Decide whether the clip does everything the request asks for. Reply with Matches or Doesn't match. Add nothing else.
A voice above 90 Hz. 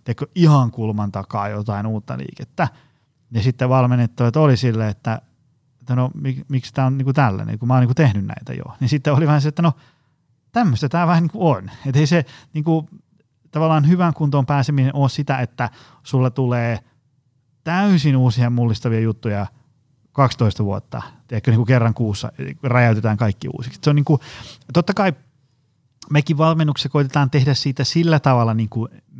Matches